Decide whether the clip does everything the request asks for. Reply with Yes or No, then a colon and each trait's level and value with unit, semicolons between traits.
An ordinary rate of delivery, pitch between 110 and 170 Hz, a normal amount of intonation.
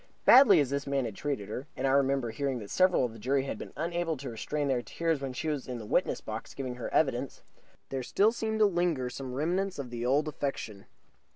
No: fast, 235 wpm; medium, 140 Hz; average, 4.3 semitones